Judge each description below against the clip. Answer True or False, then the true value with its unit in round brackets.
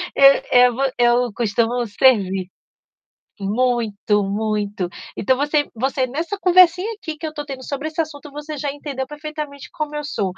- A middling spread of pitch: True (4.9 semitones)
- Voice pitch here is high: True (265 Hz)